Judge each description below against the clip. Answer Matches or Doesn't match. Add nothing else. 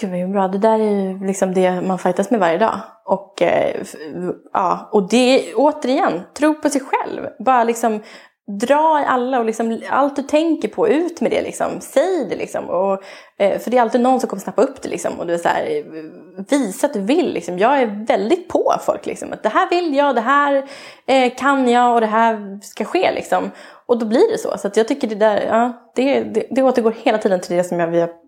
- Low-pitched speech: Doesn't match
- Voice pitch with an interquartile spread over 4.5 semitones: Matches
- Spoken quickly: Matches